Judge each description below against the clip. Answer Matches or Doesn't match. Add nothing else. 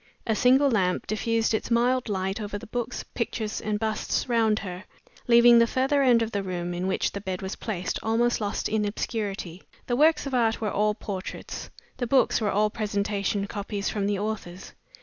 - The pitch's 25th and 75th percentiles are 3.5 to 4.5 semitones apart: Doesn't match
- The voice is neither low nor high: Doesn't match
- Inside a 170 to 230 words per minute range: Matches